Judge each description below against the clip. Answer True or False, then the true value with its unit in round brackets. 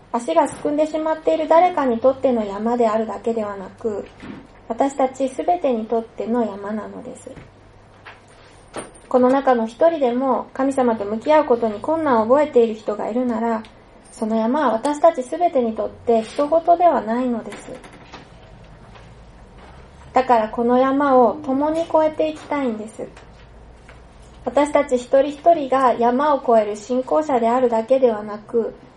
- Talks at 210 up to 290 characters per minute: False (300 characters per minute)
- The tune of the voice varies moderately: True (4.1 semitones)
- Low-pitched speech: False (250 Hz)